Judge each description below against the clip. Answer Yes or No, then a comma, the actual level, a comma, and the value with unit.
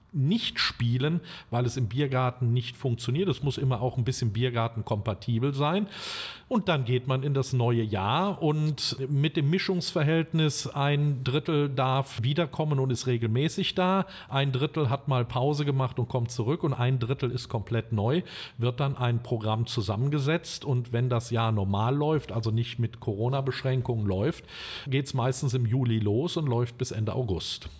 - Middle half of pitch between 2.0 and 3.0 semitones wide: No, average, 3.8 semitones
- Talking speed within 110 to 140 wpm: No, average, 170 wpm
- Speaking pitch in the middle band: No, low, 130 Hz